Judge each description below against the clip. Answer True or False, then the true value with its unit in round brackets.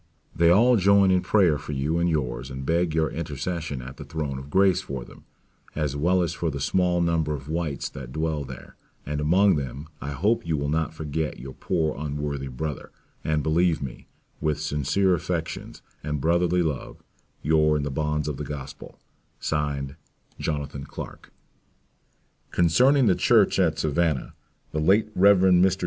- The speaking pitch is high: False (75 Hz)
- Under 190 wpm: True (170 wpm)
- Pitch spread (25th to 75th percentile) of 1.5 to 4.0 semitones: True (3.4 semitones)